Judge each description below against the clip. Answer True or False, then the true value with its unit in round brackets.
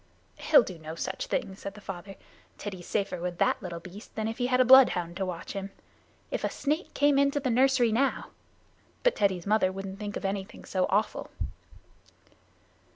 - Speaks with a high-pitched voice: True (200 Hz)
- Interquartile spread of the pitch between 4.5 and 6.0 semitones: True (5.2 semitones)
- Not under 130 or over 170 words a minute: False (190 wpm)